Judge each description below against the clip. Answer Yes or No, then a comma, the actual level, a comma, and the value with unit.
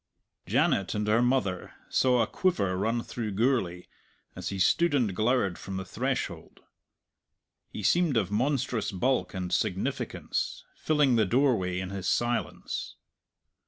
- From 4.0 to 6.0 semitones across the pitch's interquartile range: Yes, average, 5.2 semitones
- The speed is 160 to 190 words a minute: No, slow, 135 wpm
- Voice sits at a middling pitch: No, low, 110 Hz